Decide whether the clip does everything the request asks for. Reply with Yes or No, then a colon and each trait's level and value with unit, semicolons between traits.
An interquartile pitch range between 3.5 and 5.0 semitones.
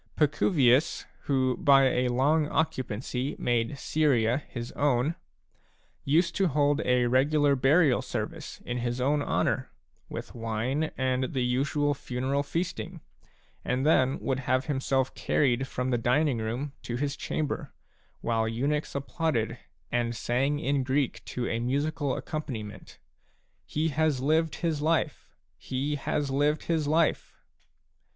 No: average, 3.1 semitones